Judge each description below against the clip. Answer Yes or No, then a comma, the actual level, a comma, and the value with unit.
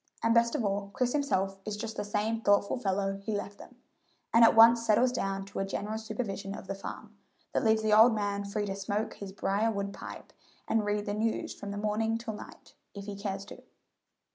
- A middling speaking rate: No, fast, 215 wpm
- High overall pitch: Yes, high, 210 Hz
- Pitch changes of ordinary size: No, narrow, 2.0 semitones